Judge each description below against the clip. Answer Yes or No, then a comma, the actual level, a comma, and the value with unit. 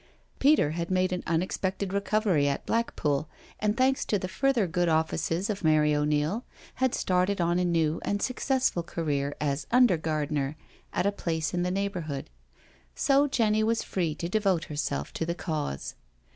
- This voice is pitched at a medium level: Yes, medium, 175 Hz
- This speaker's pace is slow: No, average, 170 wpm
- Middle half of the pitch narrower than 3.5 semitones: No, average, 5.0 semitones